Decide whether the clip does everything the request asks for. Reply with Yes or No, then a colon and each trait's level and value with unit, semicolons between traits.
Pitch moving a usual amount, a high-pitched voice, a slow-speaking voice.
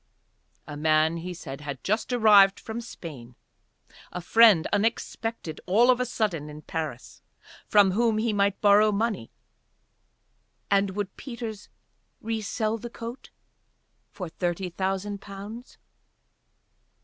Yes: average, 4.8 semitones; high, 200 Hz; slow, 120 wpm